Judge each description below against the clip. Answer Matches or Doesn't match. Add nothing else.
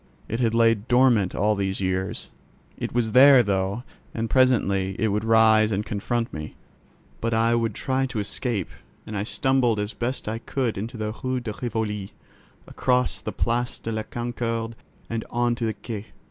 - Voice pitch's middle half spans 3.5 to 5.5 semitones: Doesn't match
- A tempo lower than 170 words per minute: Doesn't match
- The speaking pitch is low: Matches